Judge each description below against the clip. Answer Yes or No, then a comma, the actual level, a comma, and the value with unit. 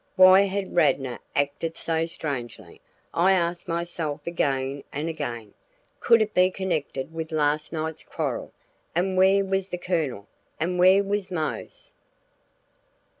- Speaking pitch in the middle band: Yes, medium, 165 Hz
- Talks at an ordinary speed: No, slow, 130 wpm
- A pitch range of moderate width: Yes, average, 4.2 semitones